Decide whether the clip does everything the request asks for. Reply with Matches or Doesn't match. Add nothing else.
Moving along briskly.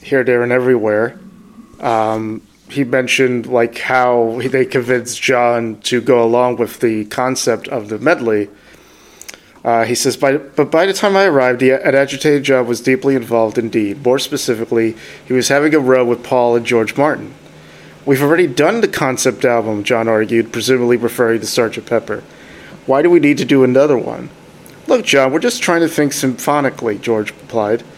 Doesn't match